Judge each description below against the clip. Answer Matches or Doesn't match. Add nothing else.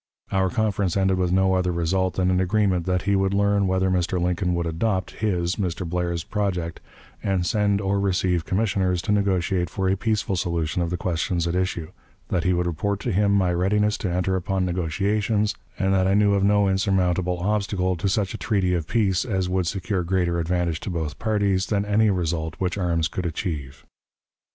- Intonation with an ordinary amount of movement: Doesn't match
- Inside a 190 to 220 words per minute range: Matches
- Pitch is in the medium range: Doesn't match